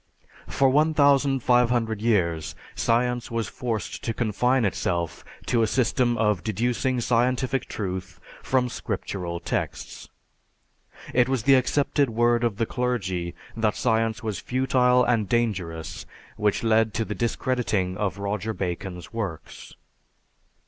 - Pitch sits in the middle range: No, low, 115 Hz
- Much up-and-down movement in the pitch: No, average, 3.7 semitones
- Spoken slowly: Yes, slow, 120 wpm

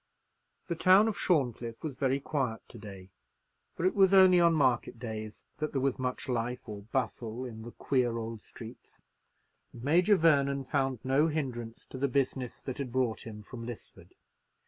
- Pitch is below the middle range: Yes, low, 130 Hz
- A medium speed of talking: Yes, average, 175 wpm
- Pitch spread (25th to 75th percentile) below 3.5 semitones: No, average, 4.0 semitones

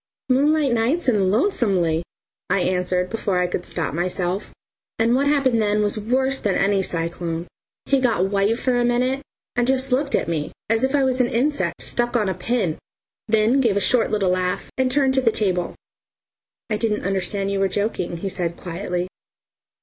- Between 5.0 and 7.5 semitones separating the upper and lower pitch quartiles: Yes, wide, 5.6 semitones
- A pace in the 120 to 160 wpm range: No, average, 185 wpm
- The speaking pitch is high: Yes, high, 215 Hz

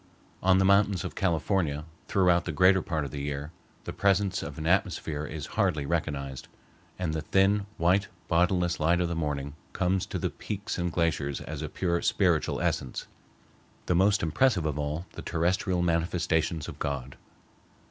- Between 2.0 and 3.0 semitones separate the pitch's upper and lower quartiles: No, average, 3.7 semitones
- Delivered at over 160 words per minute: Yes, average, 170 wpm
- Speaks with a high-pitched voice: No, very low, 85 Hz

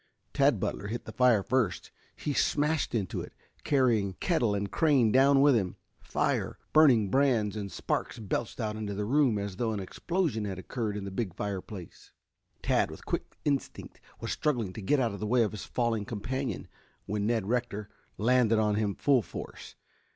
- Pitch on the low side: Yes, low, 110 Hz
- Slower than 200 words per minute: Yes, average, 180 wpm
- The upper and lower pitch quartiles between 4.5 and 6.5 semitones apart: No, average, 4.1 semitones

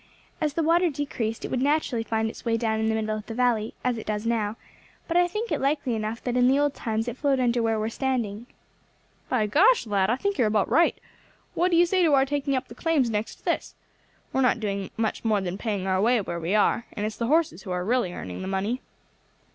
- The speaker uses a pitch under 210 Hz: No, high, 235 Hz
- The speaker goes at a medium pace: No, fast, 255 wpm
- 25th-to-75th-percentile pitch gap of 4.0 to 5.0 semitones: Yes, average, 4.5 semitones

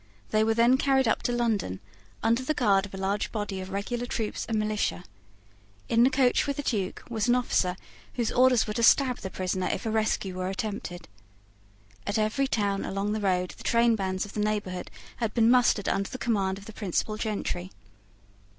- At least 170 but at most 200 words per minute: Yes, average, 195 wpm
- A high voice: Yes, high, 215 Hz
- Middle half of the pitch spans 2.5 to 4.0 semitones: Yes, average, 3.4 semitones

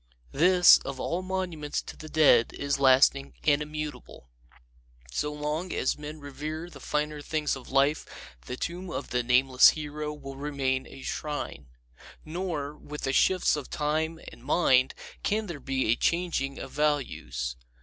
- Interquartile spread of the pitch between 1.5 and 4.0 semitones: Yes, narrow, 2.6 semitones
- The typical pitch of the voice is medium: Yes, medium, 150 Hz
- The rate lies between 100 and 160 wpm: Yes, average, 155 wpm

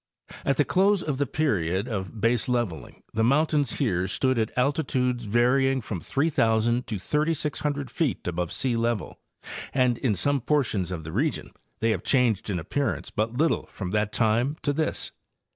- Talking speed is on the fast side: No, average, 160 wpm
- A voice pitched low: Yes, low, 120 Hz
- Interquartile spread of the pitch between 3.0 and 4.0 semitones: No, average, 4.8 semitones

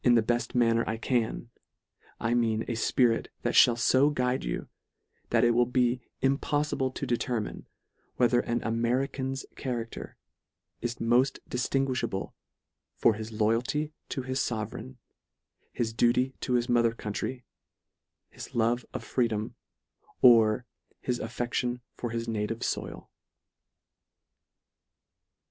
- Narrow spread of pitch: Yes, narrow, 1.7 semitones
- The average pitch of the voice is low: Yes, low, 120 Hz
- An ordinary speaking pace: No, slow, 125 wpm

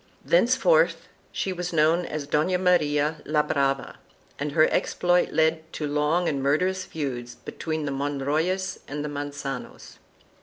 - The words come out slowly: No, average, 145 wpm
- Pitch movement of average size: Yes, average, 3.6 semitones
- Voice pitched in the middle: Yes, medium, 150 Hz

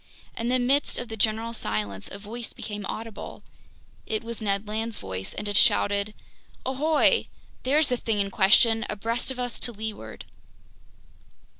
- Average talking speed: Yes, average, 155 wpm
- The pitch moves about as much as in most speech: Yes, average, 3.0 semitones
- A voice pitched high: Yes, high, 225 Hz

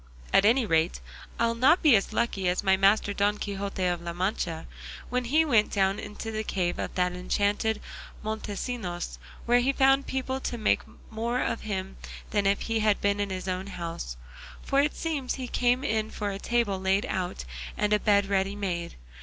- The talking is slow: No, average, 190 wpm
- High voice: Yes, high, 205 Hz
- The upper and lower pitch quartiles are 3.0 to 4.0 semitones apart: Yes, average, 3.7 semitones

